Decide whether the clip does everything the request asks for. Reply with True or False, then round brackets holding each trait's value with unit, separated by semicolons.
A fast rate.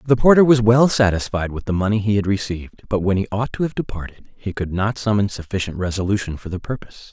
True (230 wpm)